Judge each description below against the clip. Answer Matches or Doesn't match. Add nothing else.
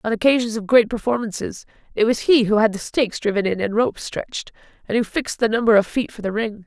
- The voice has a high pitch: Matches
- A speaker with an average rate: Doesn't match